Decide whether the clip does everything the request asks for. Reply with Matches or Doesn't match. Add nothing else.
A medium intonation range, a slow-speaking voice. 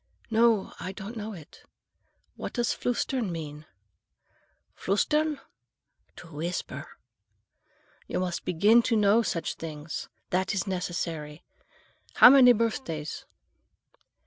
Doesn't match